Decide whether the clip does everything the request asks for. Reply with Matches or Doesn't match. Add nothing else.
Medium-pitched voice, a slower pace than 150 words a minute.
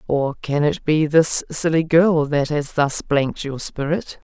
Doesn't match